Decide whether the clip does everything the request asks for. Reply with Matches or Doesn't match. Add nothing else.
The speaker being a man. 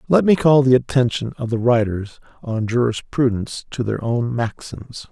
Matches